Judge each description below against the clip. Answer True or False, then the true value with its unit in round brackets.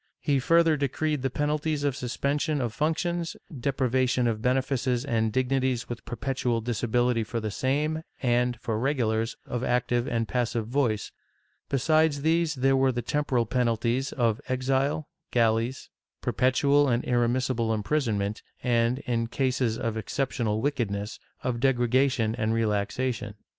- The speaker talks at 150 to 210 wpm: False (140 wpm)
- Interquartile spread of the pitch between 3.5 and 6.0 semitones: False (3.0 semitones)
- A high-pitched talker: False (125 Hz)